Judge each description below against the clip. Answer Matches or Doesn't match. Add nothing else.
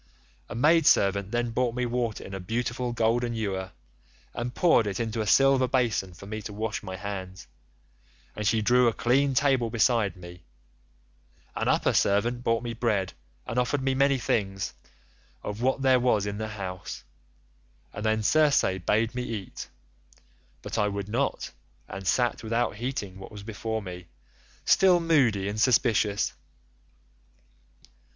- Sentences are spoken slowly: Doesn't match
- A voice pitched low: Matches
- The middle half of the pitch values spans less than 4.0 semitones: Matches